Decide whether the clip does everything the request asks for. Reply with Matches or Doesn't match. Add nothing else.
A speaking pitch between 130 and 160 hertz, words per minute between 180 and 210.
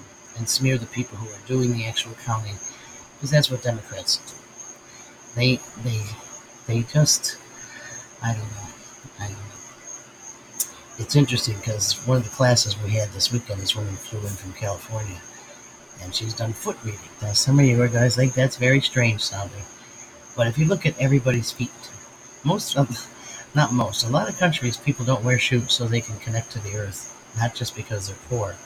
Doesn't match